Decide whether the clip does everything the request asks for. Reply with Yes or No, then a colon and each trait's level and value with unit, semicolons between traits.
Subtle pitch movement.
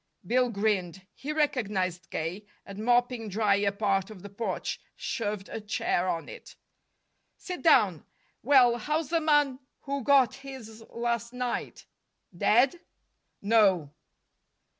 No: average, 4.6 semitones